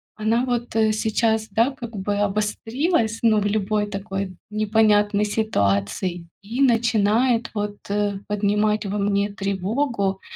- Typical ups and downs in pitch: No, narrow, 1.9 semitones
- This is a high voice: Yes, high, 210 Hz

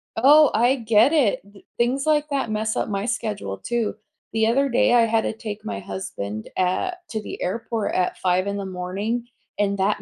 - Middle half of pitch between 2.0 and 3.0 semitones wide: No, average, 3.5 semitones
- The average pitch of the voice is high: Yes, high, 220 Hz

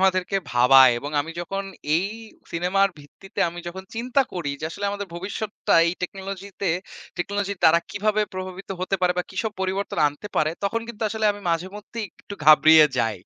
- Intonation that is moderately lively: Yes, average, 3.1 semitones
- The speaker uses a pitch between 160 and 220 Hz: Yes, high, 190 Hz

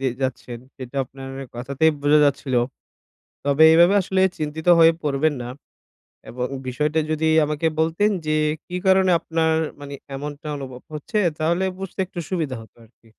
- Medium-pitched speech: Yes, medium, 150 Hz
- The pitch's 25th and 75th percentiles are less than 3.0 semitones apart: No, average, 3.3 semitones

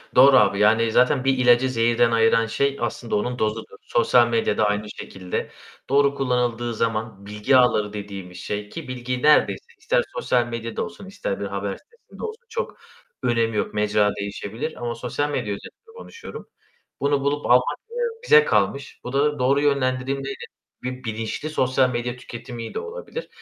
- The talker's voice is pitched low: Yes, low, 120 Hz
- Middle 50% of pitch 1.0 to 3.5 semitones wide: No, average, 4.0 semitones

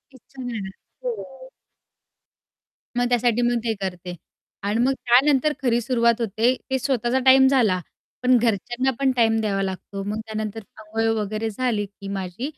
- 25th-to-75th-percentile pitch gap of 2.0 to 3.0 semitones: No, average, 3.4 semitones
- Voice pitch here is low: No, high, 235 Hz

